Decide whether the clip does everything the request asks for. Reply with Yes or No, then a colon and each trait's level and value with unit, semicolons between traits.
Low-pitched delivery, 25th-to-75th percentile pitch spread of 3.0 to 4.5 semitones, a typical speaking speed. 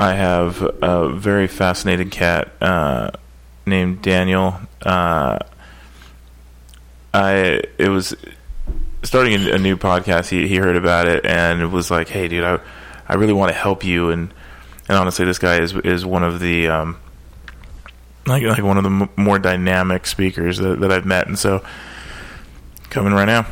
Yes: very low, 90 Hz; average, 3.7 semitones; average, 165 wpm